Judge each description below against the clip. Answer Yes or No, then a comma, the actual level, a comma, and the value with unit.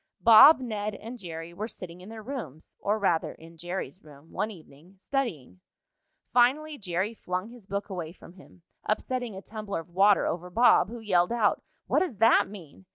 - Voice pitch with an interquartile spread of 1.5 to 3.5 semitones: No, average, 4.7 semitones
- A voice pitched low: No, high, 200 Hz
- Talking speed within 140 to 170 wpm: No, average, 180 wpm